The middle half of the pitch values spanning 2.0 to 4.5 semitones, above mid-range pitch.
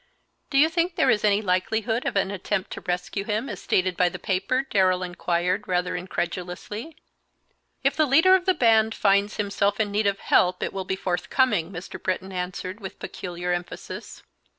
Yes: average, 3.4 semitones; high, 195 Hz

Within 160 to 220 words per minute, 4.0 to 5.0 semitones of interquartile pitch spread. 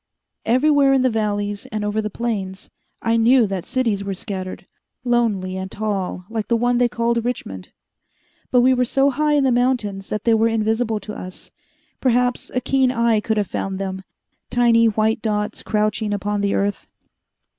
No: average, 175 wpm; average, 3.1 semitones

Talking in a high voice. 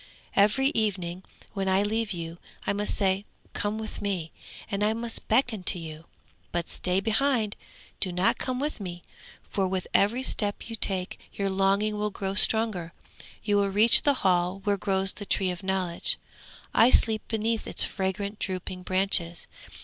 Yes: high, 200 Hz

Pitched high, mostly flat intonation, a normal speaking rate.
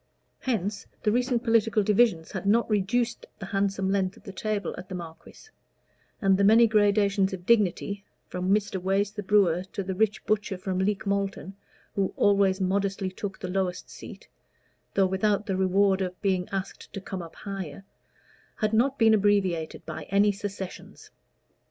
Yes: high, 200 Hz; narrow, 1.8 semitones; average, 165 wpm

